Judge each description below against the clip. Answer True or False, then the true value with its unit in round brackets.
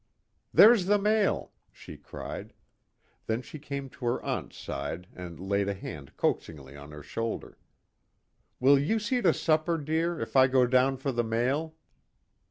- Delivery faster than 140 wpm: True (160 wpm)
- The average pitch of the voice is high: False (130 Hz)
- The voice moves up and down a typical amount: False (8.1 semitones)